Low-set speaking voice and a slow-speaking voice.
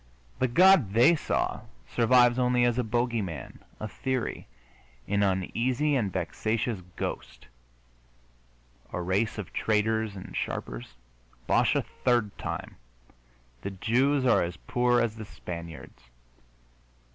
Yes: low, 115 Hz; slow, 120 wpm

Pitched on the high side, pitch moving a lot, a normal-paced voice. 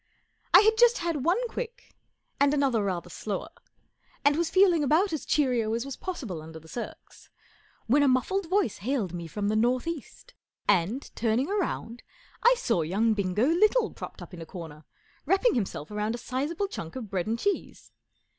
Yes: very high, 255 Hz; wide, 9.0 semitones; average, 180 wpm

